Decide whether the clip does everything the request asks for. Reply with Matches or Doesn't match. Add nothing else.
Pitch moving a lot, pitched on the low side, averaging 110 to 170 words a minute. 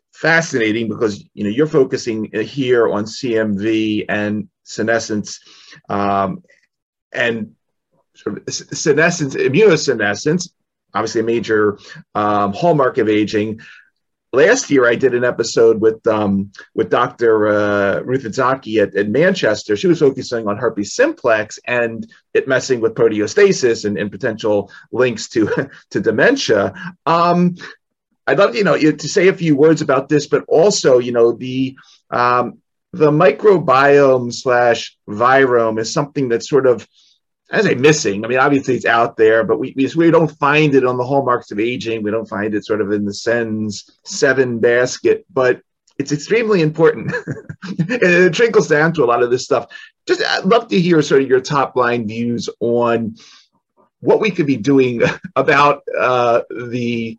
Matches